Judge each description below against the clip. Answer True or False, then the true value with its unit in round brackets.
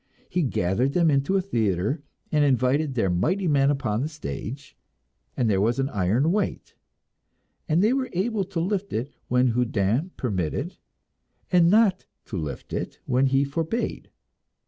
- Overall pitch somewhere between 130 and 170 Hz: True (140 Hz)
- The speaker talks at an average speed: True (155 wpm)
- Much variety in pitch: True (7.2 semitones)